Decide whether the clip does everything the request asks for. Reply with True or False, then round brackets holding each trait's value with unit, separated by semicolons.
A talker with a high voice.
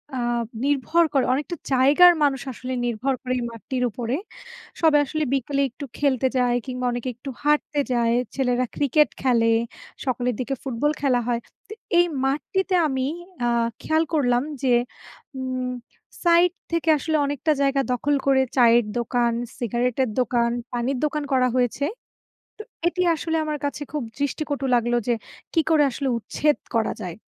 True (265 Hz)